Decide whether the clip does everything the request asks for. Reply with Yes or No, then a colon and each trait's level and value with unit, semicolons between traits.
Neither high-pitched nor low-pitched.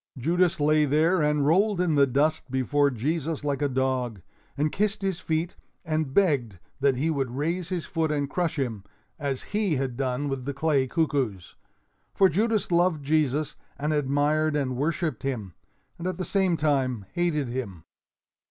Yes: medium, 150 Hz